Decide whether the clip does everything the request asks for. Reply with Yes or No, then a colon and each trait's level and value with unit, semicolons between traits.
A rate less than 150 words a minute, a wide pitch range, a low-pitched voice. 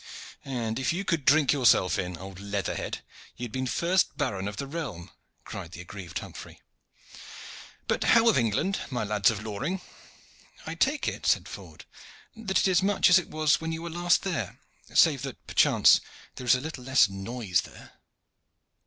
No: average, 180 wpm; wide, 8.6 semitones; low, 130 Hz